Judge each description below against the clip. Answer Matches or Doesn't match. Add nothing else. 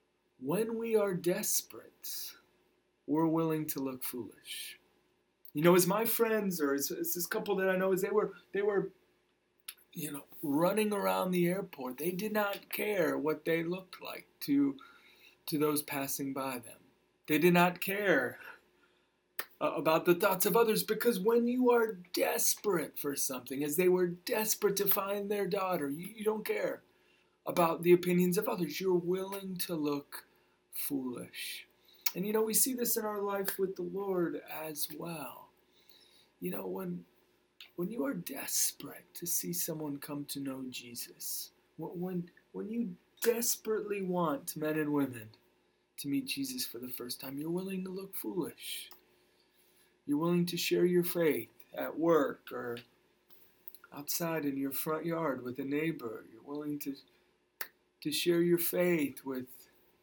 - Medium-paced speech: Matches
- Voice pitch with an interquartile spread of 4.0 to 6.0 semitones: Matches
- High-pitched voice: Doesn't match